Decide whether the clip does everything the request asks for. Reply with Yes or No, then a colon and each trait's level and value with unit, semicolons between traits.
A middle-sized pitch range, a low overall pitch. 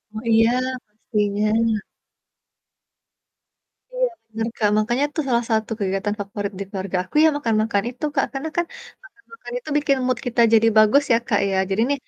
No: average, 4.8 semitones; high, 225 Hz